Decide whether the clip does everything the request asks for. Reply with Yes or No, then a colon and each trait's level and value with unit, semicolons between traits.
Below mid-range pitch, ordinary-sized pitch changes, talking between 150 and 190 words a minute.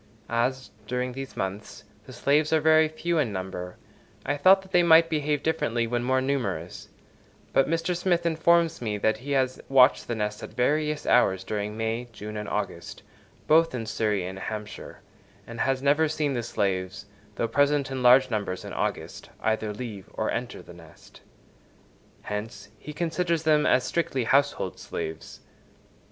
No: low, 125 Hz; wide, 6.1 semitones; average, 165 wpm